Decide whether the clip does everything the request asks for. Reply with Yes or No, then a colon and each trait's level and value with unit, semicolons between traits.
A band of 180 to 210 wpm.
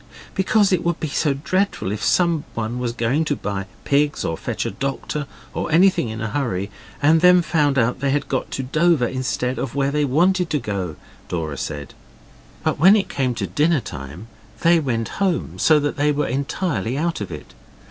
Yes: average, 195 wpm